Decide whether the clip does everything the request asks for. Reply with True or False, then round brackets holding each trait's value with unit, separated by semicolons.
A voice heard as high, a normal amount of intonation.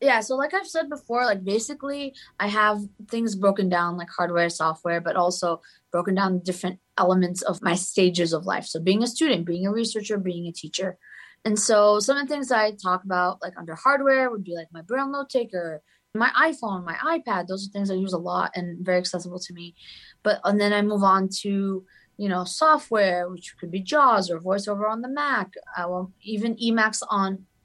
True (195 Hz; 4.0 semitones)